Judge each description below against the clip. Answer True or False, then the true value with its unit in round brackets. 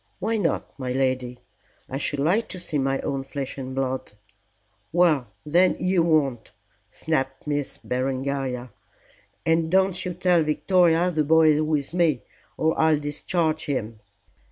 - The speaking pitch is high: False (150 Hz)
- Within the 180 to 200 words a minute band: False (145 wpm)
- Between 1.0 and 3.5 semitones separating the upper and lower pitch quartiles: False (4.0 semitones)